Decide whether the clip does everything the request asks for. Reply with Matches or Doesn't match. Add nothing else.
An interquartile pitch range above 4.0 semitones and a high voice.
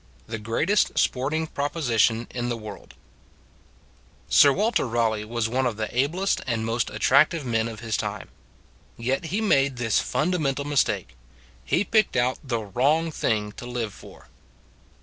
Doesn't match